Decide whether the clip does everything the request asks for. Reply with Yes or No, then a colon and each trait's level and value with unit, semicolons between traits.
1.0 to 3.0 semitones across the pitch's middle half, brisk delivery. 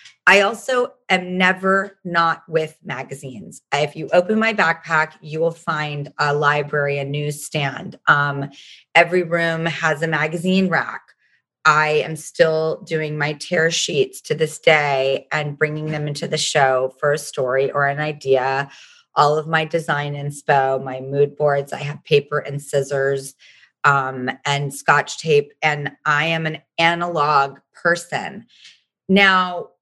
No: narrow, 2.6 semitones; average, 145 wpm